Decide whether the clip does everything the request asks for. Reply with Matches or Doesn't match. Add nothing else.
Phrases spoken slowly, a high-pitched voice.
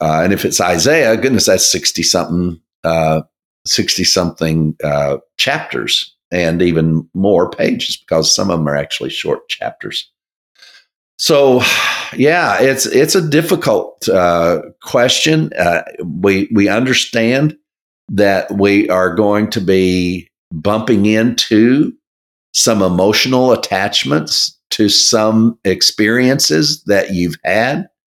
Doesn't match